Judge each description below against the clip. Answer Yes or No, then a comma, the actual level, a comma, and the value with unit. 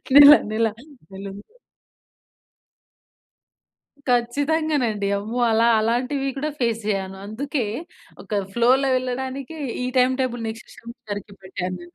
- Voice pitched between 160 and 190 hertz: No, high, 235 Hz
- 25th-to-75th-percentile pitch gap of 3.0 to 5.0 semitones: Yes, average, 3.7 semitones